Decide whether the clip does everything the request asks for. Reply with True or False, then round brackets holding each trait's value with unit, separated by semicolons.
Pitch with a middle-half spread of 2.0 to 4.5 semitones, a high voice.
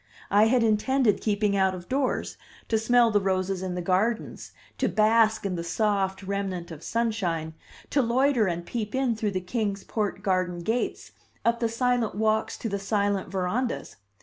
True (3.4 semitones; 210 Hz)